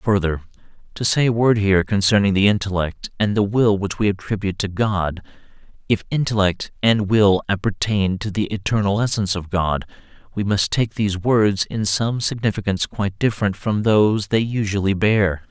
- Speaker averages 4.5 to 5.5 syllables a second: No, 4.3 syllables/s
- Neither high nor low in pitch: No, low, 100 Hz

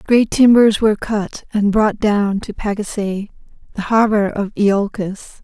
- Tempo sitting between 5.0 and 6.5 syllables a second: No, 4.3 syllables/s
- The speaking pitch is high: Yes, high, 210 Hz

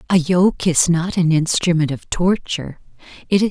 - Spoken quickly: No, average, 170 wpm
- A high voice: No, medium, 170 Hz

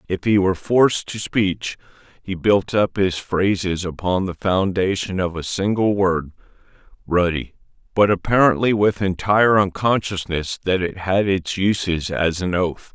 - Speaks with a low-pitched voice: Yes, very low, 95 Hz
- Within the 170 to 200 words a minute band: No, average, 150 wpm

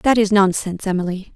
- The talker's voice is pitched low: No, high, 195 Hz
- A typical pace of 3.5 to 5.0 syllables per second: No, 6.1 syllables/s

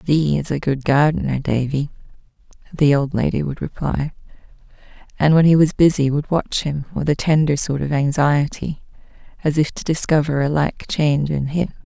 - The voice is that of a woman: Yes, female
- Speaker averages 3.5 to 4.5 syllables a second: No, 5.0 syllables/s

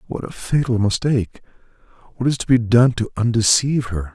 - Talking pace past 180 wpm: No, average, 175 wpm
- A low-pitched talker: Yes, low, 115 Hz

